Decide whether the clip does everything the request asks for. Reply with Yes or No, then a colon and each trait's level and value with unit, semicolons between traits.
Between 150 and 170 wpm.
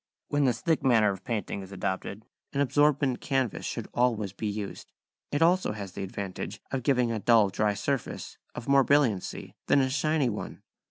No: average, 180 wpm